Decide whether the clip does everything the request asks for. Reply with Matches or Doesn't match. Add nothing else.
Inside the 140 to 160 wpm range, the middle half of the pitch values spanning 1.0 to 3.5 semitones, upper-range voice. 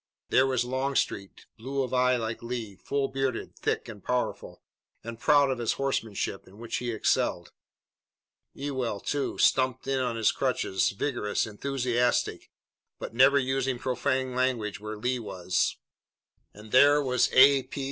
Doesn't match